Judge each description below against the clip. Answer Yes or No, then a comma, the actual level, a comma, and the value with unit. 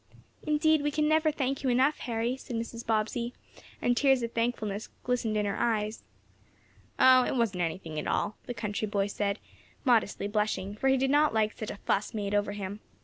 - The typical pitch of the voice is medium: No, high, 230 Hz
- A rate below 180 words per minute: No, average, 195 wpm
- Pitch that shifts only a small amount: No, average, 3.9 semitones